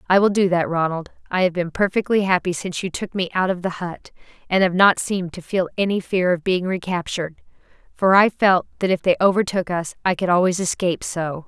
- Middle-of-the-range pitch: Yes, medium, 180 Hz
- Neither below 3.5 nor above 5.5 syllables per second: No, 5.8 syllables/s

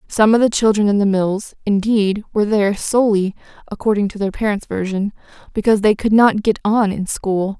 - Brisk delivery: No, average, 175 wpm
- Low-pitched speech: No, high, 205 Hz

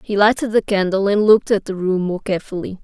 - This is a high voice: Yes, high, 200 Hz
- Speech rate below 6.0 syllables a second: No, 6.3 syllables/s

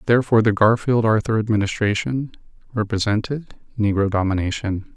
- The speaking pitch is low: Yes, low, 110 Hz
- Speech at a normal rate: No, slow, 95 wpm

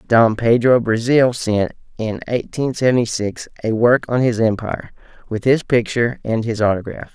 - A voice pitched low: Yes, low, 115 Hz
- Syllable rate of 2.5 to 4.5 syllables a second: No, 5.1 syllables/s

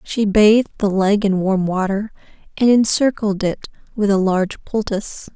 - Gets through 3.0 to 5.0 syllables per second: Yes, 4.8 syllables/s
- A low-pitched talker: No, high, 205 Hz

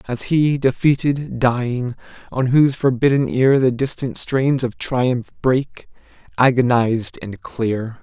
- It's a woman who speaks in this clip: No, male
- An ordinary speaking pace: No, slow, 125 wpm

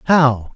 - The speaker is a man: Yes, male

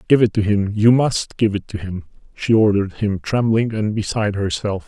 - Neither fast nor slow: No, fast, 210 wpm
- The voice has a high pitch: No, low, 105 Hz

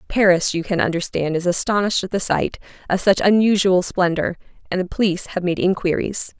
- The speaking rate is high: No, average, 180 wpm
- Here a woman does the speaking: Yes, female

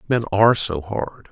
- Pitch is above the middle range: No, low, 105 Hz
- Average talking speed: Yes, average, 180 wpm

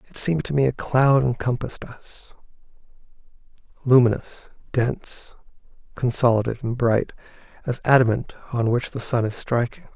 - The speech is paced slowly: Yes, slow, 125 wpm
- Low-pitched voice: Yes, low, 125 Hz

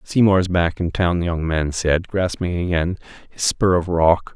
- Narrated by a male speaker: Yes, male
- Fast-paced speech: No, average, 195 wpm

